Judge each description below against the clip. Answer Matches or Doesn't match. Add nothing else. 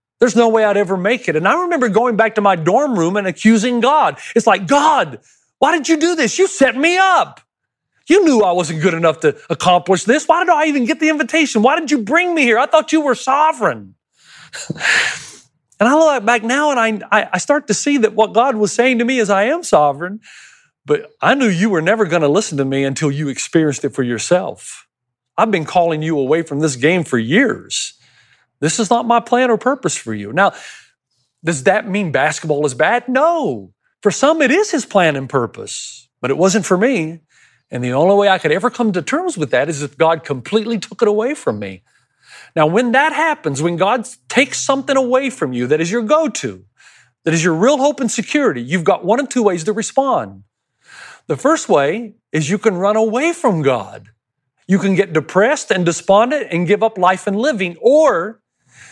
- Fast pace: Matches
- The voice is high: Matches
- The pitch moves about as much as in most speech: Doesn't match